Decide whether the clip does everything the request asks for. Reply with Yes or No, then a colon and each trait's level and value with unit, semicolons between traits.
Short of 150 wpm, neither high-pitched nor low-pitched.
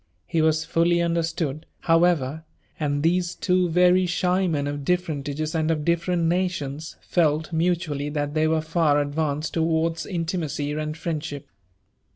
Yes: average, 140 wpm; medium, 160 Hz